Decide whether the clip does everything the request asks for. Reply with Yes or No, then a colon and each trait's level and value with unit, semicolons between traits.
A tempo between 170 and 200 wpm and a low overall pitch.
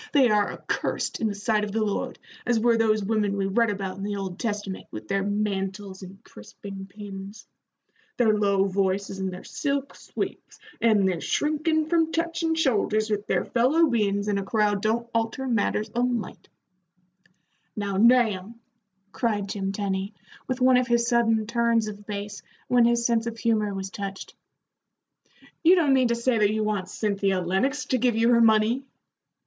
No: average, 175 wpm; high, 215 Hz